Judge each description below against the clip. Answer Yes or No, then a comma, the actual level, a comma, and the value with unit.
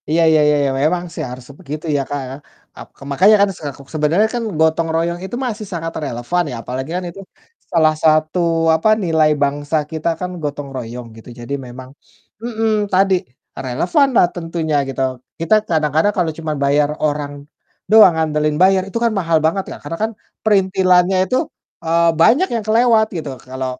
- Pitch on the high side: No, medium, 160 Hz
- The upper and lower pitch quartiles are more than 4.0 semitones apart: Yes, average, 4.4 semitones